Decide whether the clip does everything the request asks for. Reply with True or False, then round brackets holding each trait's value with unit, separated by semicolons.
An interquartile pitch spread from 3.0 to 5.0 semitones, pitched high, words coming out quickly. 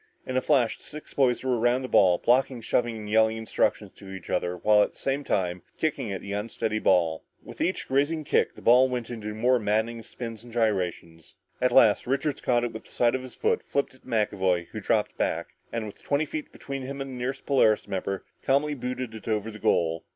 False (3.9 semitones; 115 Hz; 230 wpm)